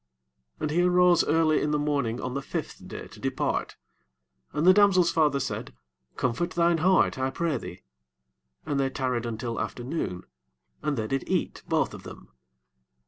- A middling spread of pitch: Yes, average, 4.9 semitones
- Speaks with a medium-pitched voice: Yes, medium, 145 Hz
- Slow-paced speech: No, average, 170 wpm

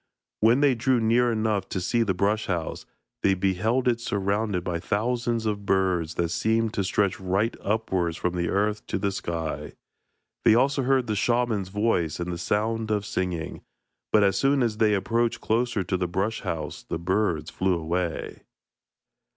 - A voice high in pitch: No, low, 100 Hz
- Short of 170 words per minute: No, average, 175 wpm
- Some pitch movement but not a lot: Yes, average, 3.9 semitones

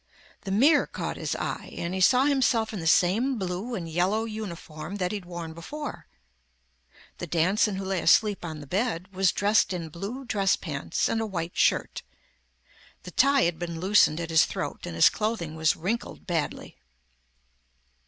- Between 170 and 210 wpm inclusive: Yes, average, 175 wpm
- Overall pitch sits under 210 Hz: Yes, high, 190 Hz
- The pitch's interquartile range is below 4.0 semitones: No, average, 4.5 semitones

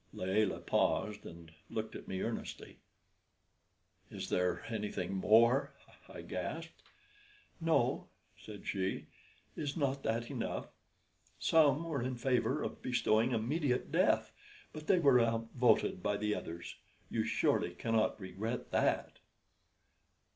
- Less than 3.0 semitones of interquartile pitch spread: No, average, 4.3 semitones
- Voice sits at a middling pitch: No, low, 115 Hz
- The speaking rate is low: Yes, slow, 120 wpm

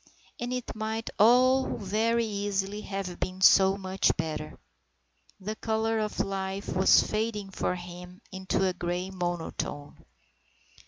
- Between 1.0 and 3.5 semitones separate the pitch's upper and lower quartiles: Yes, average, 2.9 semitones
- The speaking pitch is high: Yes, high, 195 Hz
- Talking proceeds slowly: Yes, slow, 125 wpm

